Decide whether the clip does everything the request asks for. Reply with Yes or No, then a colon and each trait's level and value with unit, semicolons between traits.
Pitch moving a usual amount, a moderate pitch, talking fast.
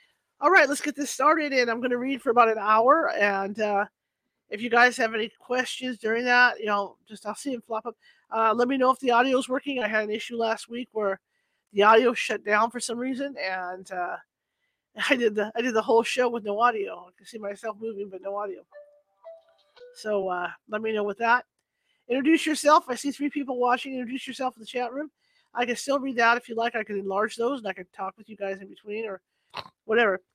No: average, 3.8 semitones; high, 235 Hz; fast, 235 wpm